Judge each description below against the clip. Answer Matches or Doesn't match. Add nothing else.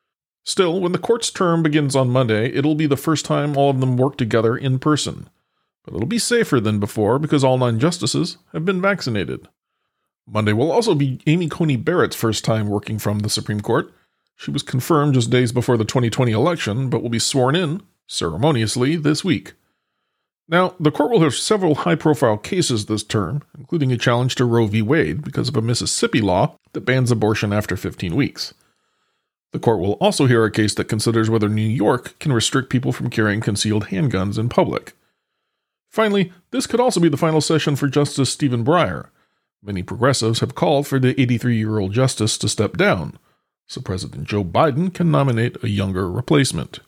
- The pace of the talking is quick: Doesn't match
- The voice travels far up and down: Matches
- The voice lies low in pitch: Matches